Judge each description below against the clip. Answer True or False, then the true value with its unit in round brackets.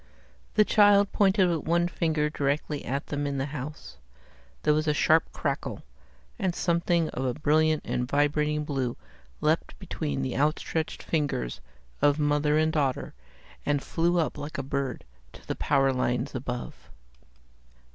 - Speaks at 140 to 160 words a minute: True (155 wpm)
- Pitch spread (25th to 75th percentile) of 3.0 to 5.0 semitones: False (2.6 semitones)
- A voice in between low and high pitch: True (150 Hz)